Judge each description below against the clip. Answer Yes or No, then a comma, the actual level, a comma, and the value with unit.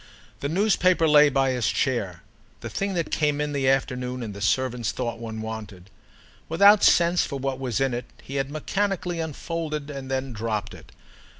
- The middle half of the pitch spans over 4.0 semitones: Yes, average, 5.0 semitones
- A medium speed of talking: Yes, average, 175 wpm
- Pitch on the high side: No, low, 135 Hz